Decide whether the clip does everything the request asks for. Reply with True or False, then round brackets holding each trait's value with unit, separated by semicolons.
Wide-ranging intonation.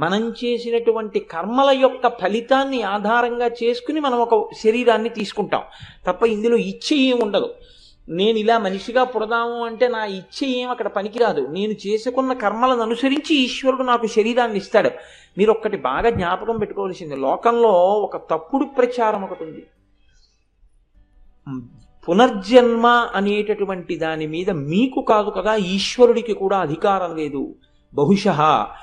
False (3.9 semitones)